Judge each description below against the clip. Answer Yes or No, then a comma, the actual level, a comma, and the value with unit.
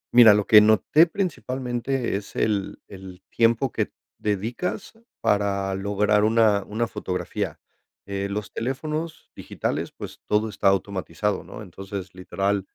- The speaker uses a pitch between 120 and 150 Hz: No, low, 105 Hz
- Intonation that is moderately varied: Yes, average, 3.1 semitones